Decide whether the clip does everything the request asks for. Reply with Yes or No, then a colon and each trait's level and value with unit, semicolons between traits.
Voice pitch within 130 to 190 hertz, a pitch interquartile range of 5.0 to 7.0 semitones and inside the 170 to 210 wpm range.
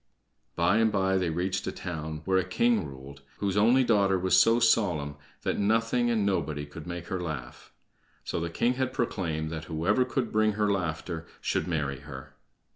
No: very low, 95 Hz; wide, 5.4 semitones; average, 185 wpm